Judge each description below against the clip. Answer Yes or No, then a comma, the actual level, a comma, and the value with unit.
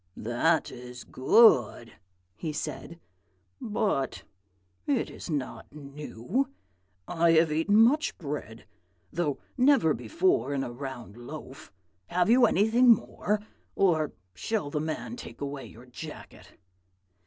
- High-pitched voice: No, medium, 155 Hz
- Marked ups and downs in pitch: Yes, wide, 7.9 semitones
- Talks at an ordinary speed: No, slow, 120 wpm